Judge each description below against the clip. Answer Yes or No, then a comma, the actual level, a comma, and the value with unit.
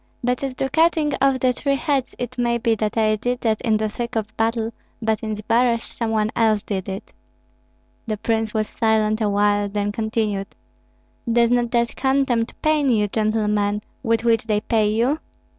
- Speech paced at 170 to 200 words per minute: Yes, average, 180 wpm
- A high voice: Yes, high, 225 Hz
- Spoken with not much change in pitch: Yes, narrow, 2.3 semitones